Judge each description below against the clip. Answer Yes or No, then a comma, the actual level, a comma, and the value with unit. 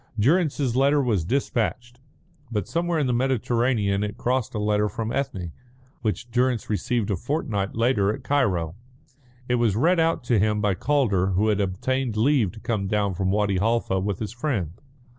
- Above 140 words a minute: Yes, average, 175 wpm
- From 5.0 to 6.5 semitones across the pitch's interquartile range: No, average, 4.3 semitones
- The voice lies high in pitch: No, low, 115 Hz